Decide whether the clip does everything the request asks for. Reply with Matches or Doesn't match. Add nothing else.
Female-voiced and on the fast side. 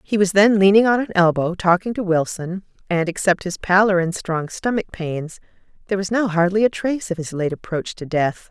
Matches